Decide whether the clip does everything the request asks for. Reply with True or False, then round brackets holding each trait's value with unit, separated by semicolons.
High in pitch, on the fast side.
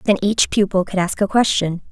True (195 Hz; 220 wpm)